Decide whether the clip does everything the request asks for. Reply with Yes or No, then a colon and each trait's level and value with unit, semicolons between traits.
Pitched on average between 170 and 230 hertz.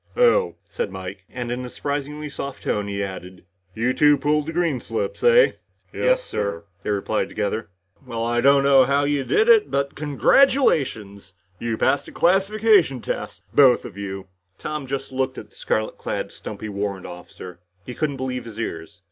No: low, 130 Hz